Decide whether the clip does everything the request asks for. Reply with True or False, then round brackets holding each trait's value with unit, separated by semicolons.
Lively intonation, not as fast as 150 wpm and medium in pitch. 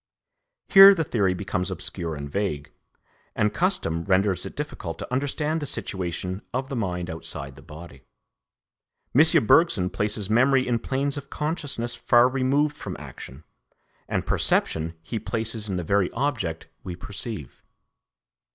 False (7.3 semitones; 140 wpm; 105 Hz)